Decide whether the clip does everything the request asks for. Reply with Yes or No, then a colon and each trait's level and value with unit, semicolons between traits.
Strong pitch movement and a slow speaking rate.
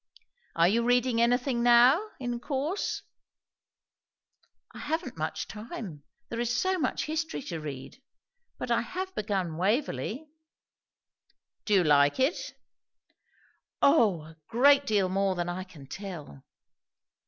Yes: wide, 7.1 semitones; slow, 125 wpm